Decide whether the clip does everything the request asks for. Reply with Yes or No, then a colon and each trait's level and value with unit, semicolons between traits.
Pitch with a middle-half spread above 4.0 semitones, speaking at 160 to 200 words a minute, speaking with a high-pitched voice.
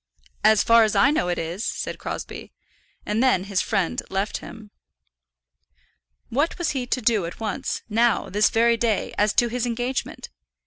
No: average, 3.0 semitones; average, 170 wpm; high, 225 Hz